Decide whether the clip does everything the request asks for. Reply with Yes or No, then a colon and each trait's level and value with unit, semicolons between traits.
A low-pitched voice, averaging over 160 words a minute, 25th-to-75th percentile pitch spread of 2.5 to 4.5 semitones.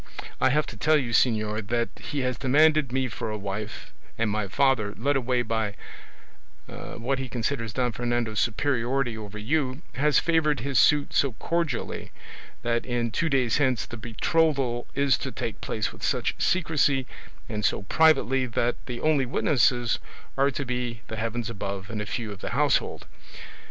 Yes: low, 120 Hz; average, 170 wpm; average, 3.8 semitones